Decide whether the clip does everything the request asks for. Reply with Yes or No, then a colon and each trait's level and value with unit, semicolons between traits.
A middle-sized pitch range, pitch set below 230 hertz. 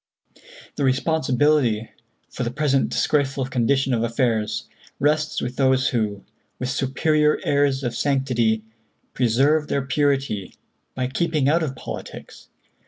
Yes: average, 3.0 semitones; low, 135 Hz